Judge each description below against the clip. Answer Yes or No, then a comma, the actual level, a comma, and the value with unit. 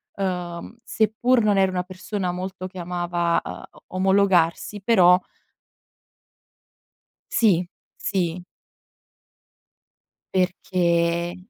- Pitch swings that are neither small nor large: No, narrow, 1.9 semitones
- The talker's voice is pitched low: No, medium, 185 Hz